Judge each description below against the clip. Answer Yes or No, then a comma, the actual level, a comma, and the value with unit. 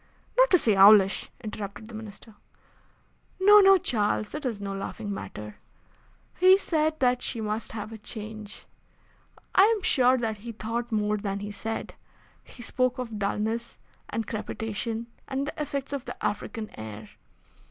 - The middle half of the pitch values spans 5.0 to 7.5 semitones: No, average, 3.6 semitones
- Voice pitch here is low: No, high, 225 Hz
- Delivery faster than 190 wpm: No, average, 155 wpm